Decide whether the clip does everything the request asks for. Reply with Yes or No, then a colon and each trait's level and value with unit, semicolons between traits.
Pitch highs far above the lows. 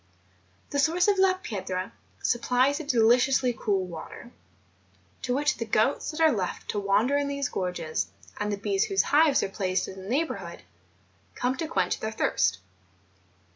Yes: wide, 6.6 semitones